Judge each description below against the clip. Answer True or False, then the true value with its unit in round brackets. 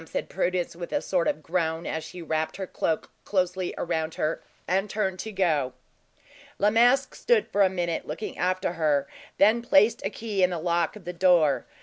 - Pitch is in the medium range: True (180 Hz)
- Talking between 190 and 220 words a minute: True (200 wpm)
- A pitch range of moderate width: True (3.3 semitones)